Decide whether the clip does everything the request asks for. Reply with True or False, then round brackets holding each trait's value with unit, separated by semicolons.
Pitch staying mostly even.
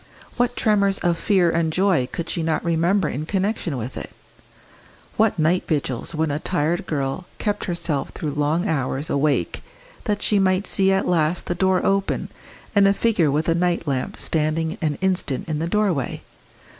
False (4.0 semitones)